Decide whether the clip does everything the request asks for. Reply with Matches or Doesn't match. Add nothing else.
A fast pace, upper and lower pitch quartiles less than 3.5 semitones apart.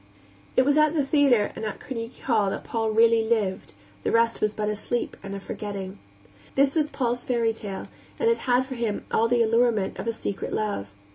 Matches